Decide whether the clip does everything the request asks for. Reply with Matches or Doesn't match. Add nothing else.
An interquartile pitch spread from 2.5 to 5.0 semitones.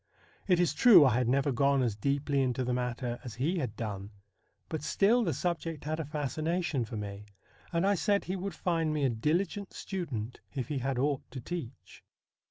Doesn't match